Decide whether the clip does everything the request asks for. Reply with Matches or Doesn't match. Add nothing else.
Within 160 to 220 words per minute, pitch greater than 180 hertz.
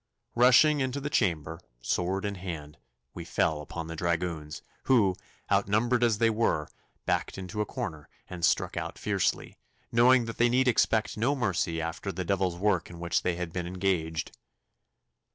Doesn't match